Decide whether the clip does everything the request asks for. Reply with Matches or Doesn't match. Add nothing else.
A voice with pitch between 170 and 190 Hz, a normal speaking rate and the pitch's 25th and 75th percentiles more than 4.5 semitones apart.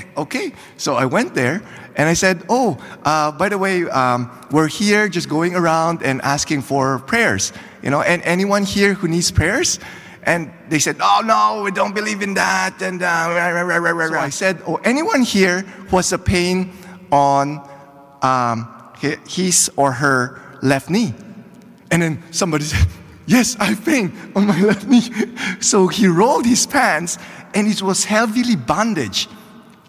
Matches